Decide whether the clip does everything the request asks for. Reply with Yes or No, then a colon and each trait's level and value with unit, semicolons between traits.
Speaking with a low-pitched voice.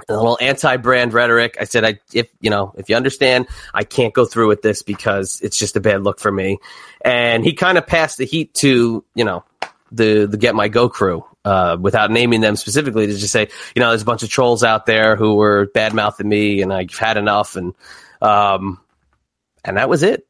Yes: low, 110 Hz